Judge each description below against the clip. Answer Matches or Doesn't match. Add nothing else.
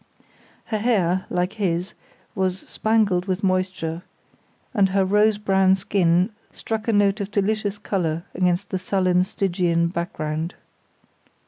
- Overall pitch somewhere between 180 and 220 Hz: Matches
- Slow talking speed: Matches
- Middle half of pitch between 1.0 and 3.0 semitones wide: Matches